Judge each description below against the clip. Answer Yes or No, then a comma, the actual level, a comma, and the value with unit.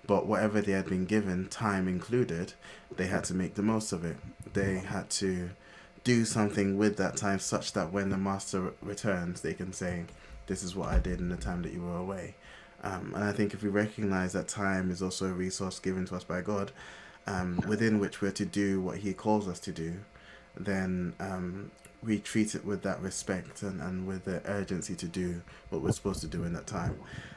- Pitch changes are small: Yes, narrow, 1.8 semitones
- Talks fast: Yes, fast, 215 wpm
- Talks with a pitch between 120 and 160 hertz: No, very low, 95 Hz